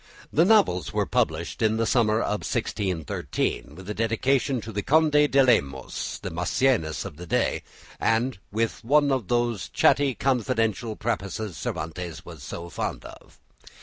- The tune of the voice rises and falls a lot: Yes, wide, 6.6 semitones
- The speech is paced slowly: No, average, 150 wpm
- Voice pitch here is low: Yes, low, 110 Hz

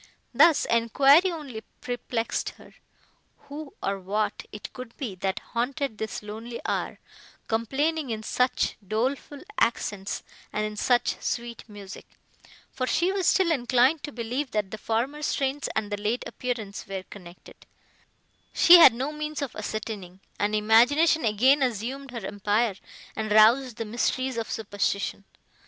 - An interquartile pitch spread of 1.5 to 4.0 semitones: No, average, 4.5 semitones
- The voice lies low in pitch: No, high, 235 Hz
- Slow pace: No, average, 145 wpm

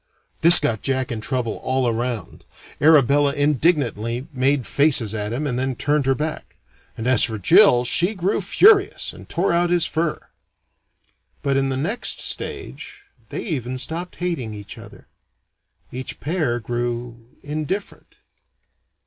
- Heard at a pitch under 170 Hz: Yes, low, 135 Hz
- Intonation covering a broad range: No, average, 5.0 semitones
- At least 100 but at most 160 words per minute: Yes, average, 140 wpm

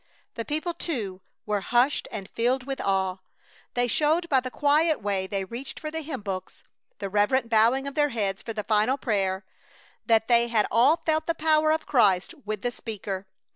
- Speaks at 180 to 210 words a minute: Yes, average, 190 wpm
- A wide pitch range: Yes, wide, 6.0 semitones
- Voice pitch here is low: No, high, 235 Hz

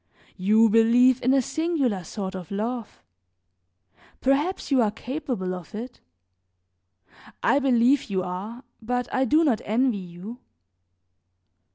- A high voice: Yes, high, 235 Hz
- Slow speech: Yes, slow, 125 wpm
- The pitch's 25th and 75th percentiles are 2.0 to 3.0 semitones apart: No, average, 4.5 semitones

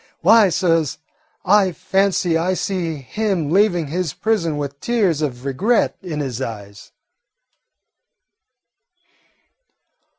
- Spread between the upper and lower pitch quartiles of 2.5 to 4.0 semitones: No, average, 5.2 semitones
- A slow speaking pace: Yes, slow, 100 wpm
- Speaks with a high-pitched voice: No, medium, 170 Hz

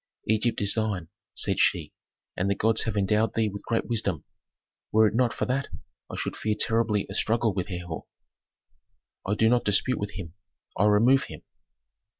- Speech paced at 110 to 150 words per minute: No, average, 175 wpm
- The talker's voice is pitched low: Yes, low, 110 Hz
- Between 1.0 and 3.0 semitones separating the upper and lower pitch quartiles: Yes, narrow, 2.4 semitones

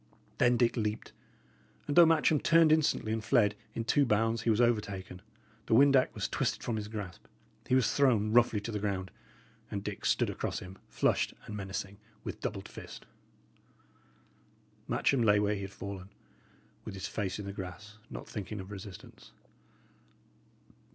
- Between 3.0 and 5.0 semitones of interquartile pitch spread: Yes, average, 3.3 semitones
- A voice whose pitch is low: Yes, low, 105 Hz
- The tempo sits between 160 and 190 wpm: Yes, average, 165 wpm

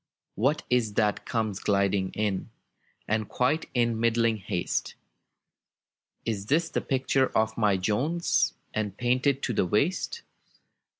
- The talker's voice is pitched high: No, low, 110 Hz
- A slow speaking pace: Yes, slow, 125 wpm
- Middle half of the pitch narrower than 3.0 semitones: No, average, 3.8 semitones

